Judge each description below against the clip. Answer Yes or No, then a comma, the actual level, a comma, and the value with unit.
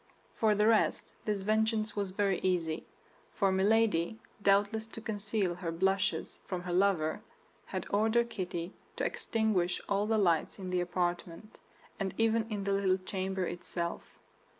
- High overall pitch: Yes, high, 195 Hz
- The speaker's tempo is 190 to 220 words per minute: No, average, 150 wpm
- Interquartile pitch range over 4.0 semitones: No, average, 3.1 semitones